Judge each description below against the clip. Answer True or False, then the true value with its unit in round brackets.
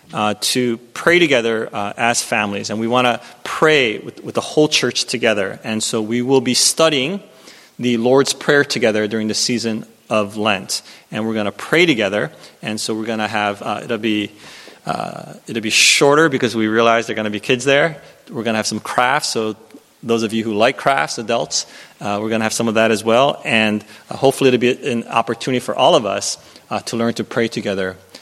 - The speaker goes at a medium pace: False (220 wpm)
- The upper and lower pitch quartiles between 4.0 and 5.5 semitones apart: False (2.5 semitones)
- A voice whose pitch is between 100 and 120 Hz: True (115 Hz)